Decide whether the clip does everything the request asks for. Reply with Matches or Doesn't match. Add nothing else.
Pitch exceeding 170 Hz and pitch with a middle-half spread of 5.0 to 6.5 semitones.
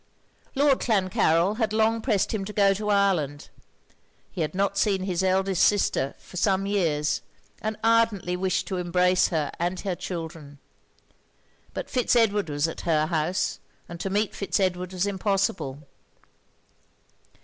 Doesn't match